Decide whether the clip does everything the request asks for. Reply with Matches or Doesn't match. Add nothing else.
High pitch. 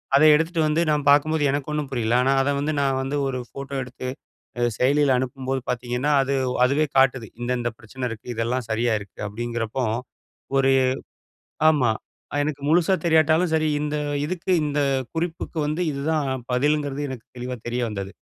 Doesn't match